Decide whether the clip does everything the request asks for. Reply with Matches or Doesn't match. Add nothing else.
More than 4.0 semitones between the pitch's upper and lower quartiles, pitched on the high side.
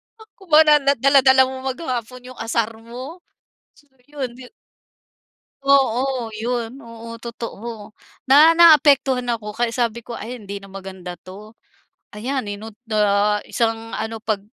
Doesn't match